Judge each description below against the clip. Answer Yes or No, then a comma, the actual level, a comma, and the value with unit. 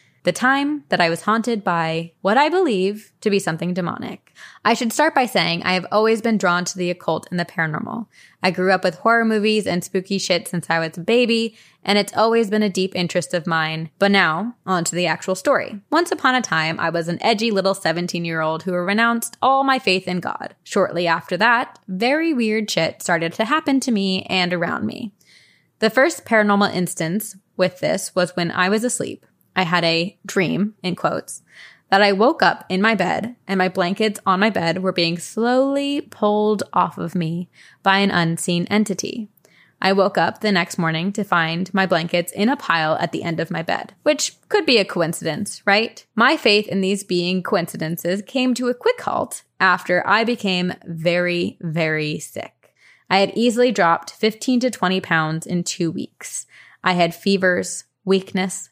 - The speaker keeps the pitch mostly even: No, average, 3.9 semitones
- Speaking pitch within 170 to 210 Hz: Yes, high, 190 Hz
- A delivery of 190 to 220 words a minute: Yes, average, 195 wpm